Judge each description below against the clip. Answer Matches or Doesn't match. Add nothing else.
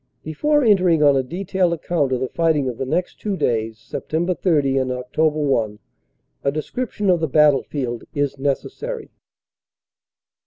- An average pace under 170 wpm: Matches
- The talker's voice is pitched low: Doesn't match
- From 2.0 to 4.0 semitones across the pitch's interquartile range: Doesn't match